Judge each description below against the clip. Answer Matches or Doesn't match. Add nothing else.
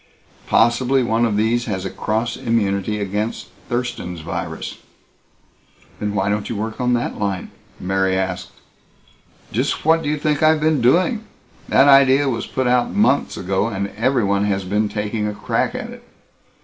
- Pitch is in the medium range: Doesn't match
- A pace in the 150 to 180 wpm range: Matches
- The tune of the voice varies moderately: Matches